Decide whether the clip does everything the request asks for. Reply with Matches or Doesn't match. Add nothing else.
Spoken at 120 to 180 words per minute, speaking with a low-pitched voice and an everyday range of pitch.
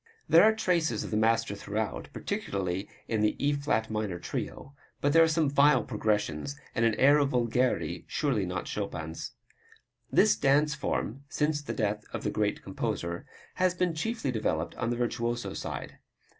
Doesn't match